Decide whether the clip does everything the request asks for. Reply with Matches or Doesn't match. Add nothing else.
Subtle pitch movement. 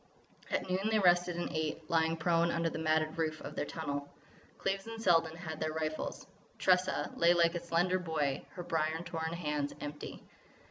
Matches